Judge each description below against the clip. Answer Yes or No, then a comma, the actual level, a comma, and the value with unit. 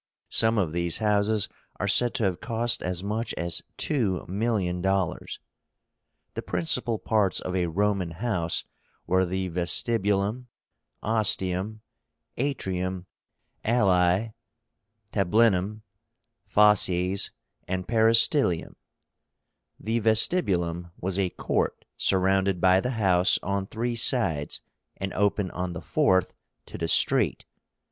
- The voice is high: No, very low, 95 Hz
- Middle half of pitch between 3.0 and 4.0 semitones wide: Yes, average, 3.5 semitones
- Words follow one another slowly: Yes, slow, 110 wpm